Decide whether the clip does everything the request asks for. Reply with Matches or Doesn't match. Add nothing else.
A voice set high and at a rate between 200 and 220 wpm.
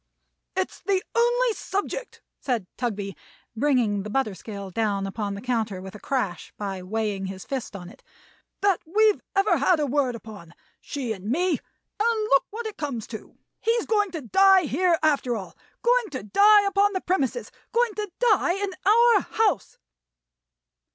Doesn't match